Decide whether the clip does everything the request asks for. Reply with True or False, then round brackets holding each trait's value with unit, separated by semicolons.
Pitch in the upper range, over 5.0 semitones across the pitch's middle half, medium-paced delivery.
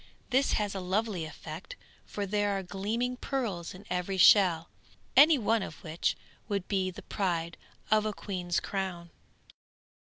False (195 Hz; 3.2 semitones; 150 wpm)